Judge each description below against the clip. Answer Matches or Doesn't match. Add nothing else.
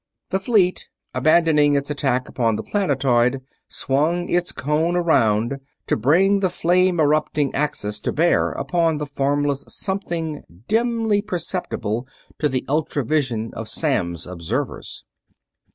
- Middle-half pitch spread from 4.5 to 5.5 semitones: Matches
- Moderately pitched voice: Matches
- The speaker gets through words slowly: Matches